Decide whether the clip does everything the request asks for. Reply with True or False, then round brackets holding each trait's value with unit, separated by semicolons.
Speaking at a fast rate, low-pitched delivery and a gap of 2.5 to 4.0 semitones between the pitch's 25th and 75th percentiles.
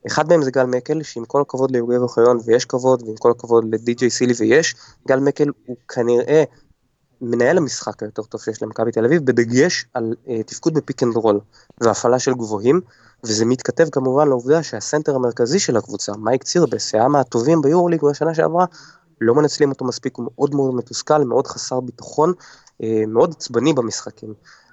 True (170 wpm; 125 Hz; 3.7 semitones)